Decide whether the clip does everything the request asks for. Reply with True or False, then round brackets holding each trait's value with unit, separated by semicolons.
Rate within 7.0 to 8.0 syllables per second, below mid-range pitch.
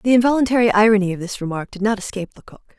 False (7.6 syllables/s; 210 Hz)